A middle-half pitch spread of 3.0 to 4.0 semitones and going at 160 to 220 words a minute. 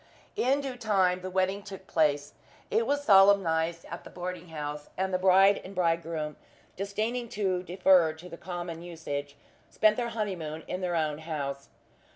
Yes: average, 3.4 semitones; average, 165 wpm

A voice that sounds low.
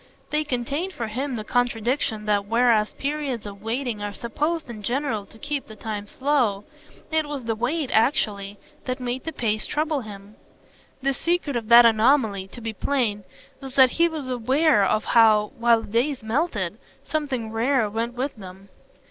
No: high, 240 Hz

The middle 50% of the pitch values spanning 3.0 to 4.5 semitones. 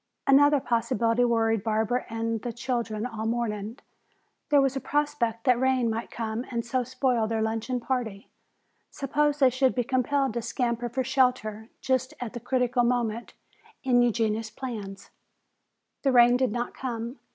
No: narrow, 2.4 semitones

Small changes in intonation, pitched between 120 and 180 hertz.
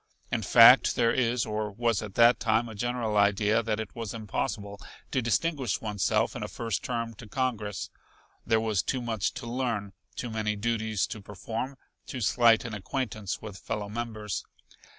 No: narrow, 2.2 semitones; low, 110 Hz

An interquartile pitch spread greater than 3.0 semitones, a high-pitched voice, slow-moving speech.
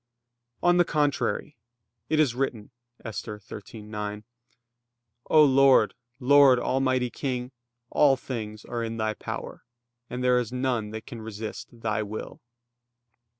No: average, 3.6 semitones; low, 125 Hz; slow, 125 wpm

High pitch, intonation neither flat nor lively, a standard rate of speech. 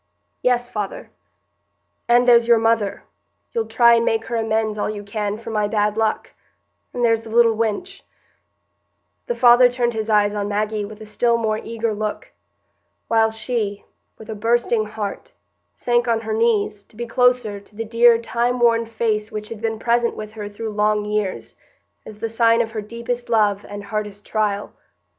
No: high, 225 Hz; narrow, 1.8 semitones; average, 175 wpm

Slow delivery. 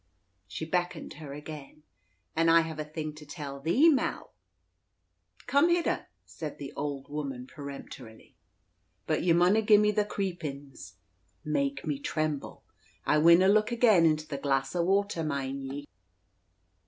No: average, 145 wpm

